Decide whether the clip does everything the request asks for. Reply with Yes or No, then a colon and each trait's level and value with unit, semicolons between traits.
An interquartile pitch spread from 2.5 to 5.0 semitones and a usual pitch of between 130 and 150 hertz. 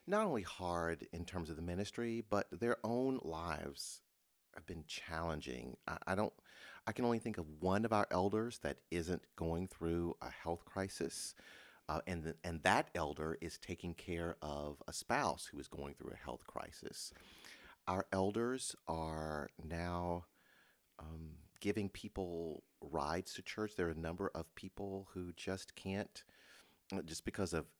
No: average, 3.4 semitones; very low, 90 Hz